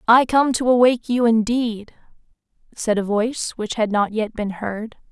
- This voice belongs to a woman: Yes, female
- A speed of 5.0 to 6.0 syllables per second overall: No, 4.7 syllables/s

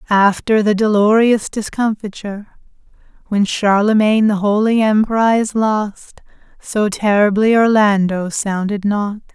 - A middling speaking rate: No, slow, 95 wpm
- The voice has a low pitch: No, high, 210 Hz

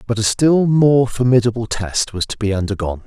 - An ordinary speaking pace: Yes, average, 195 wpm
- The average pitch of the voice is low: Yes, low, 115 Hz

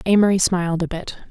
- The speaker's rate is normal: Yes, average, 185 wpm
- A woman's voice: Yes, female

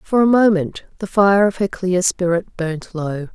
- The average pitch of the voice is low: No, medium, 185 Hz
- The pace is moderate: Yes, average, 195 wpm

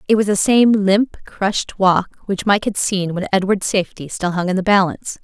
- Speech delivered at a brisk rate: Yes, fast, 220 wpm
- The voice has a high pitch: Yes, high, 195 Hz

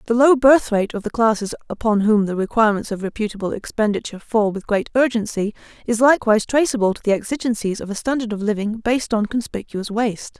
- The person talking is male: No, female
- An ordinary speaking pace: Yes, average, 185 wpm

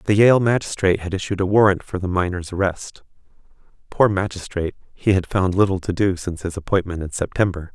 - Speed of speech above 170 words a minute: Yes, average, 180 wpm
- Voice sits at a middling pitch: No, very low, 95 Hz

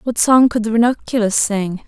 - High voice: Yes, high, 225 Hz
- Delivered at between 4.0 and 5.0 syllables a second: Yes, 4.9 syllables/s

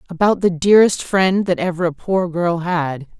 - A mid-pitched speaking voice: Yes, medium, 175 Hz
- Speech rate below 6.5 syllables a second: Yes, 4.8 syllables/s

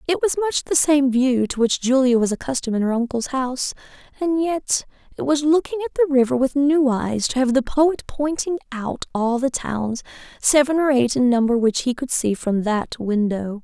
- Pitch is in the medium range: No, very high, 260 Hz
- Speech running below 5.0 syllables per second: No, 5.2 syllables/s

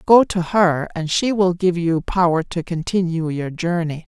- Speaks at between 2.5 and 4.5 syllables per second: Yes, 4.4 syllables/s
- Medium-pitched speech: Yes, medium, 175 Hz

